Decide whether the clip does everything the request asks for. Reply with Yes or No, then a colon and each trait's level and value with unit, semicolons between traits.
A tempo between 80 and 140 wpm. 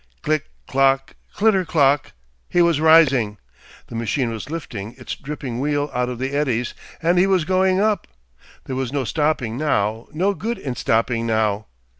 No: average, 165 wpm